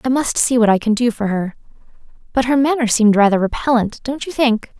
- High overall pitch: Yes, high, 235 Hz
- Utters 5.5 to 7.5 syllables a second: Yes, 5.9 syllables/s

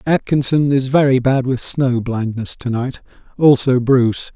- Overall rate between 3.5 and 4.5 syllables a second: Yes, 4.4 syllables/s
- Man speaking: Yes, male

